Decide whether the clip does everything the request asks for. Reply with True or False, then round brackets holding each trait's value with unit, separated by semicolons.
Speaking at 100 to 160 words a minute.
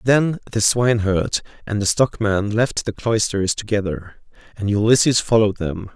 True (140 wpm)